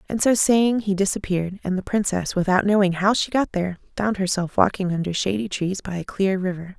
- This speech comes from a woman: Yes, female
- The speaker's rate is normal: No, fast, 210 wpm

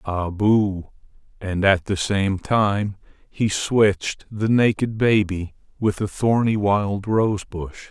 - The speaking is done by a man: Yes, male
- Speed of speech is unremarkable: No, slow, 130 wpm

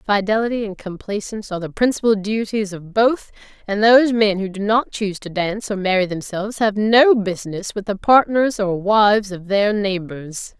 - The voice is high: Yes, high, 205 Hz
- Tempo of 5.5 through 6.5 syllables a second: No, 5.2 syllables/s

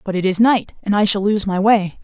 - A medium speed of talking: No, fast, 295 wpm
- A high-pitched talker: Yes, high, 200 Hz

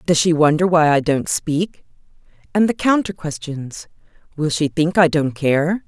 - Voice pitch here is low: No, medium, 160 Hz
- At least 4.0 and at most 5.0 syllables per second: Yes, 4.4 syllables/s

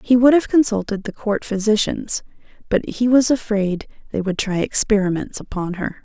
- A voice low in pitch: No, high, 215 Hz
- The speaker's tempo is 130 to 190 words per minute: Yes, average, 170 wpm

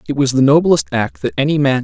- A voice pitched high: No, medium, 140 Hz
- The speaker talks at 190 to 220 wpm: No, fast, 260 wpm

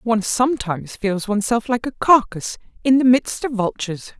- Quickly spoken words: No, average, 170 wpm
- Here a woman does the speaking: Yes, female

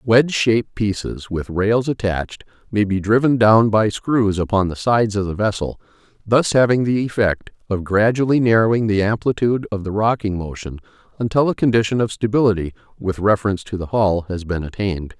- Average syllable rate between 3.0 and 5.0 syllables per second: No, 5.5 syllables/s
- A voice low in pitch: Yes, low, 105 Hz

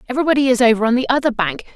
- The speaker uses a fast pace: Yes, fast, 240 wpm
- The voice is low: No, high, 245 Hz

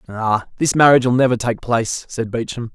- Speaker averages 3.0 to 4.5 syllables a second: No, 5.8 syllables/s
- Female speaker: No, male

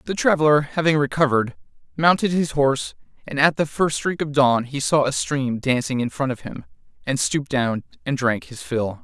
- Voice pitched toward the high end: No, medium, 140 Hz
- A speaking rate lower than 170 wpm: No, average, 200 wpm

